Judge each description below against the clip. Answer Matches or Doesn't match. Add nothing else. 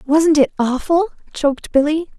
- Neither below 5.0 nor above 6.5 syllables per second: Doesn't match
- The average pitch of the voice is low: Doesn't match